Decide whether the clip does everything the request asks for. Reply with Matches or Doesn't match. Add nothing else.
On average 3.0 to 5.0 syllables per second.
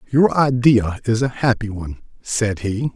Matches